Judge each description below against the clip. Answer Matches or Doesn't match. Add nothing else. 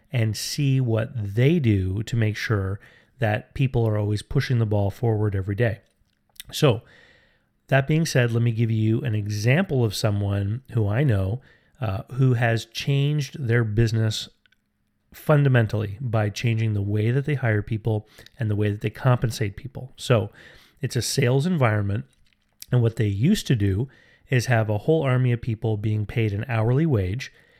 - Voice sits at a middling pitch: Doesn't match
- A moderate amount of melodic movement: Matches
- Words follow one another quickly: Doesn't match